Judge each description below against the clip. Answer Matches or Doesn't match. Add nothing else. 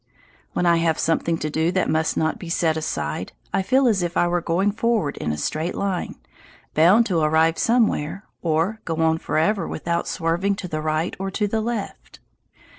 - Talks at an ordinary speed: Matches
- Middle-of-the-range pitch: Matches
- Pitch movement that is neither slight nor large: Matches